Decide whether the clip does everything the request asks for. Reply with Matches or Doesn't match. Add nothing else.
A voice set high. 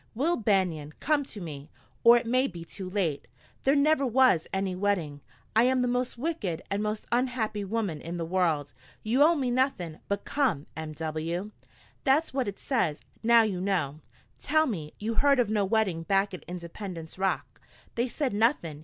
Matches